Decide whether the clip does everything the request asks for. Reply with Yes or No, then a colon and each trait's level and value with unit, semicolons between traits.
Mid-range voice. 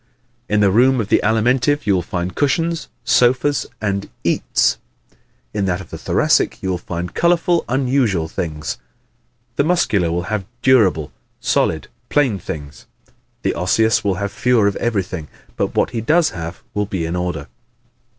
No: low, 100 Hz